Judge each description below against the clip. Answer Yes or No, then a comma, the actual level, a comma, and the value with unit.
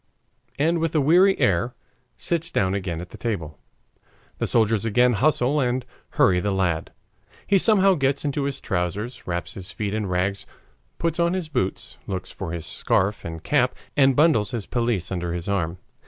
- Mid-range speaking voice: No, low, 110 Hz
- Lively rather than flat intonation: Yes, wide, 7.7 semitones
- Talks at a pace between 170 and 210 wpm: Yes, average, 175 wpm